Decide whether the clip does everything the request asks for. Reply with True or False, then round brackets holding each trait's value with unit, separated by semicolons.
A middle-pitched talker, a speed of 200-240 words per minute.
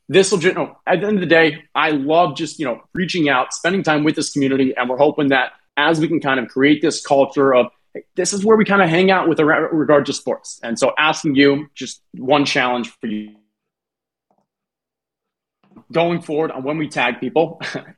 True (150 Hz; 205 wpm)